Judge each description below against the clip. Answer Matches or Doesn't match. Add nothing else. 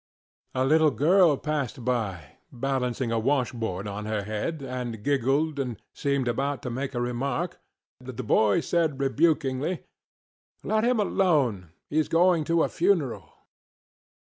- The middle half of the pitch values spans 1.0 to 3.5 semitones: Doesn't match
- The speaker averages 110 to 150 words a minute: Matches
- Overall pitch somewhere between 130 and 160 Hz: Matches